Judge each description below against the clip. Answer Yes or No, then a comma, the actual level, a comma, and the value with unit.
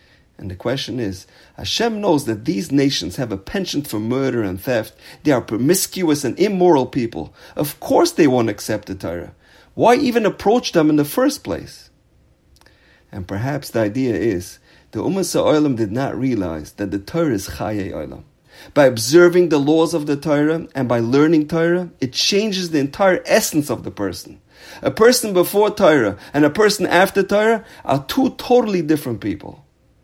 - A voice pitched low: No, medium, 155 Hz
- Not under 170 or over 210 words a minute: Yes, average, 175 wpm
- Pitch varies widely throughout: Yes, wide, 7.0 semitones